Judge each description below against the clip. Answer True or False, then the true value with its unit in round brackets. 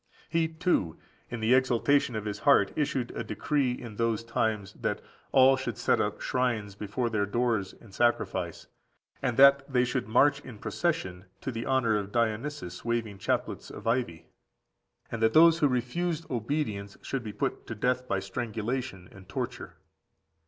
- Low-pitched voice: True (120 Hz)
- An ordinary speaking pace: True (165 wpm)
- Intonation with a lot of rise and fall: False (4.0 semitones)